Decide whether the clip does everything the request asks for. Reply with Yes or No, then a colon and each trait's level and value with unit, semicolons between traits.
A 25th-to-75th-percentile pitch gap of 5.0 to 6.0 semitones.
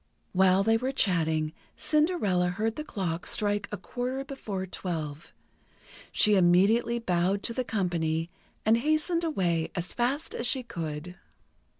Yes: wide, 5.6 semitones